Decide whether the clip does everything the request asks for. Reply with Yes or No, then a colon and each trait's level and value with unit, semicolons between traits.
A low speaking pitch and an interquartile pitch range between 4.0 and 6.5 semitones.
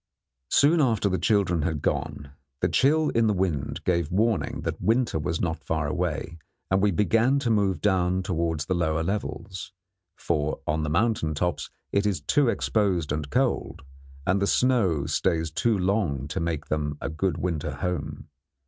Yes: very low, 90 Hz; average, 4.9 semitones